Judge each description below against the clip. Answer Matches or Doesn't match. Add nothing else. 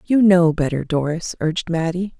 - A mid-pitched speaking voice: Matches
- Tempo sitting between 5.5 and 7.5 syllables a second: Doesn't match